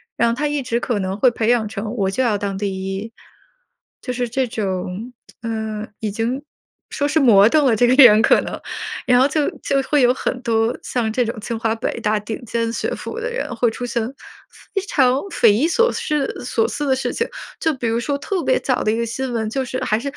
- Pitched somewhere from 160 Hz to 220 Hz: No, high, 235 Hz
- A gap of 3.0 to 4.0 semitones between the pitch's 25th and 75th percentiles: Yes, average, 3.3 semitones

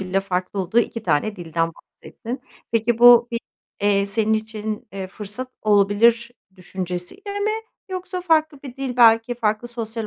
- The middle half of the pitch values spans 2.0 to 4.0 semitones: Yes, average, 3.5 semitones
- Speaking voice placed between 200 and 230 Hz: Yes, high, 220 Hz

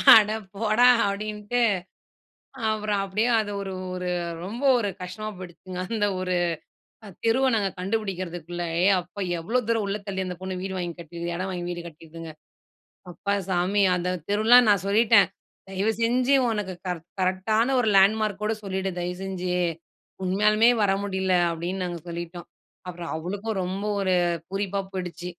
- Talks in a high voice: Yes, high, 195 Hz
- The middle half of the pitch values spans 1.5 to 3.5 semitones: Yes, average, 2.9 semitones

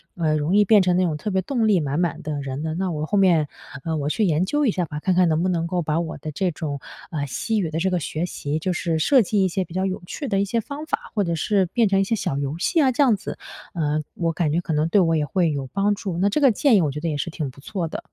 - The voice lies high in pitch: No, medium, 175 Hz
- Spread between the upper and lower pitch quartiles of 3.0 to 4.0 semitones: No, average, 4.4 semitones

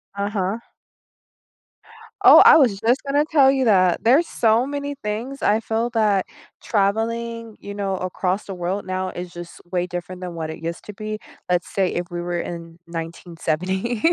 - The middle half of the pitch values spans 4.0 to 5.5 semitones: Yes, average, 4.4 semitones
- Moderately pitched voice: No, high, 200 Hz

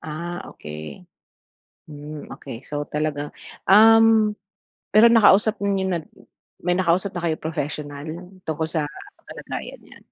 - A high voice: No, medium, 165 Hz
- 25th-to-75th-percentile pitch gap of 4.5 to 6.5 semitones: Yes, wide, 5.4 semitones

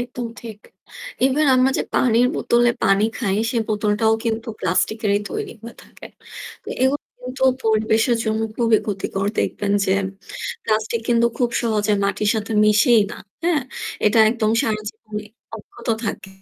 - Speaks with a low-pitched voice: No, high, 220 Hz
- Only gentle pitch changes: Yes, narrow, 2.3 semitones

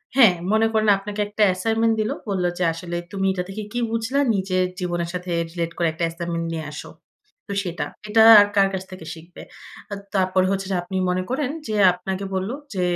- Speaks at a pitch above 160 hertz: Yes, high, 190 Hz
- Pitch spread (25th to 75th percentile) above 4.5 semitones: No, average, 3.1 semitones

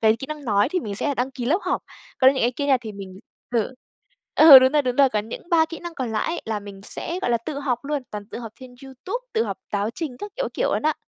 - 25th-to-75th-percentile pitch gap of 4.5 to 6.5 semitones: Yes, average, 5.2 semitones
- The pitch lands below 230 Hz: No, very high, 260 Hz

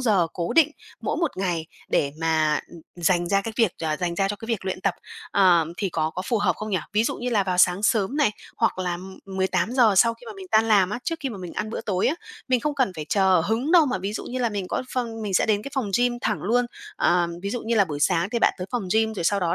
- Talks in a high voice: Yes, high, 200 Hz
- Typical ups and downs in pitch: Yes, average, 4.5 semitones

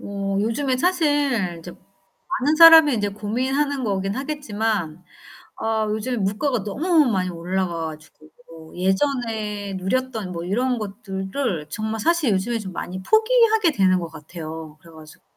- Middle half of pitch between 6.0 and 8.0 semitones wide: Yes, wide, 6.3 semitones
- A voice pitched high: Yes, high, 210 Hz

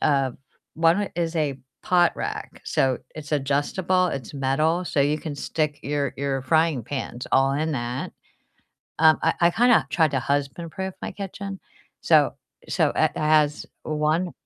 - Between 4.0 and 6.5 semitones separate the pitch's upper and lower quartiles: No, average, 3.5 semitones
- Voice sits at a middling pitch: Yes, medium, 150 Hz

